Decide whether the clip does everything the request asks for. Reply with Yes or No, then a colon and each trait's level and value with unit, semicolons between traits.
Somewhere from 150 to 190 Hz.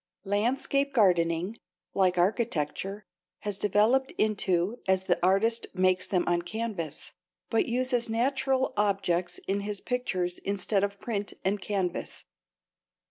No: high, 200 Hz